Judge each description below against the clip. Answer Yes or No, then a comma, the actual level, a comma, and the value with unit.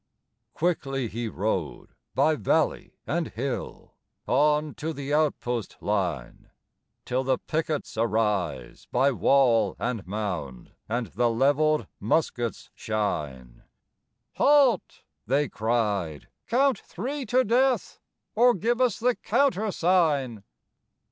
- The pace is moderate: No, slow, 105 wpm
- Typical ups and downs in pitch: No, wide, 7.3 semitones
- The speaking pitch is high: No, low, 135 Hz